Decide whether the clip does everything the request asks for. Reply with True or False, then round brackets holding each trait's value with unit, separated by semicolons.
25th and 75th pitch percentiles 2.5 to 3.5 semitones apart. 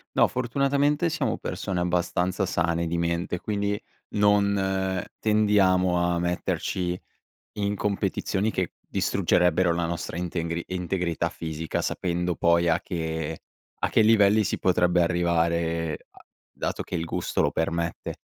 True (2.9 semitones)